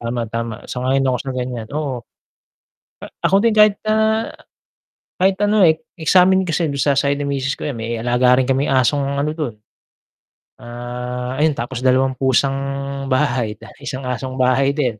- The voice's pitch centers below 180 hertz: Yes, low, 135 Hz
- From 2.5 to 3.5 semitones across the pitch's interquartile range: Yes, average, 3.1 semitones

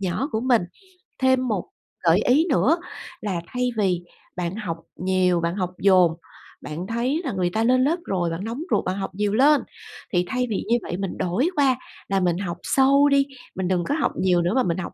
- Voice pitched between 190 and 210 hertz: Yes, high, 200 Hz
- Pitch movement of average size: No, wide, 6.2 semitones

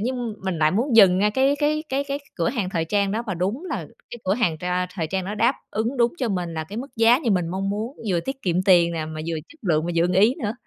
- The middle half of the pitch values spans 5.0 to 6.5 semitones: Yes, average, 5.3 semitones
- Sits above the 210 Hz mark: No, high, 200 Hz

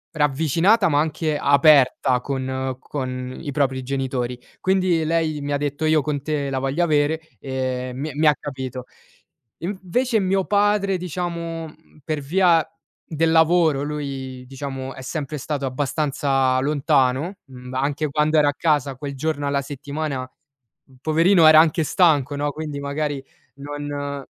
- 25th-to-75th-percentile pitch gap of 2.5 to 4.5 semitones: Yes, average, 2.9 semitones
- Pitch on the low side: No, medium, 145 Hz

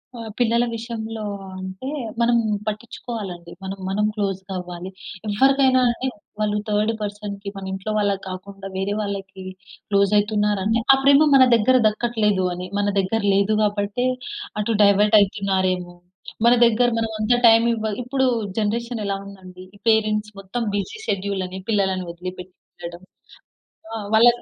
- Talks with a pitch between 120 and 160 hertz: No, high, 205 Hz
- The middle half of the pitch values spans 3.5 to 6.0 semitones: No, average, 2.8 semitones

